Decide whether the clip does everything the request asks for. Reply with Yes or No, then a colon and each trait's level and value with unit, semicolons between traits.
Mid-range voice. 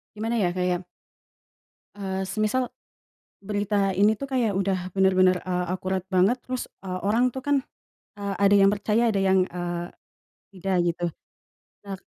No: high, 195 Hz